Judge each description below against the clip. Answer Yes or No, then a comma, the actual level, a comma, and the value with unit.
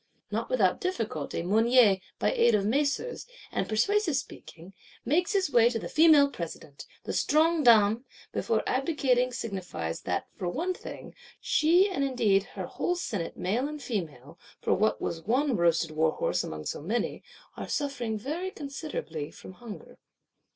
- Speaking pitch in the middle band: No, high, 240 Hz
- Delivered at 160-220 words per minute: No, average, 150 wpm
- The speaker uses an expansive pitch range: Yes, wide, 7.6 semitones